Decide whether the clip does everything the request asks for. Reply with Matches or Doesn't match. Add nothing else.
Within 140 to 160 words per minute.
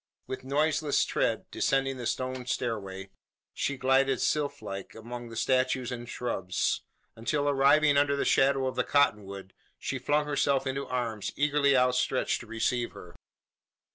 Matches